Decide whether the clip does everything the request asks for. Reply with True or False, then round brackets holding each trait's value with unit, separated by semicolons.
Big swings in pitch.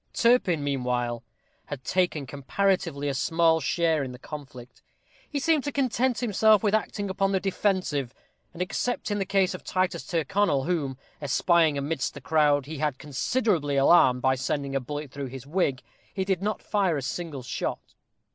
True (5.9 semitones)